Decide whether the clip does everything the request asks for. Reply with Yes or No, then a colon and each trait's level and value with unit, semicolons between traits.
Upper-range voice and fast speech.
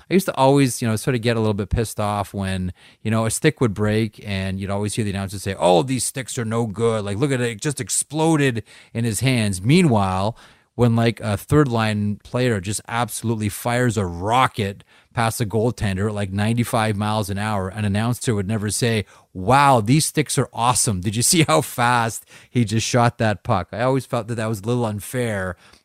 No: low, 115 Hz; fast, 220 wpm